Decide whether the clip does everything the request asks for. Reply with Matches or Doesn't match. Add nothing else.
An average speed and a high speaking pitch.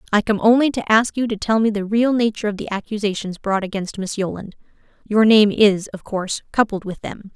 Doesn't match